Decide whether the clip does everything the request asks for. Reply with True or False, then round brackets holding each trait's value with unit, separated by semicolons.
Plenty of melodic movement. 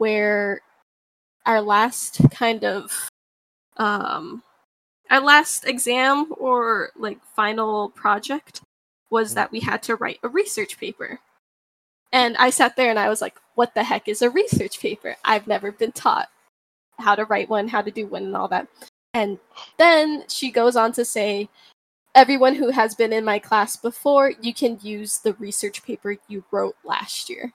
False (3.6 semitones)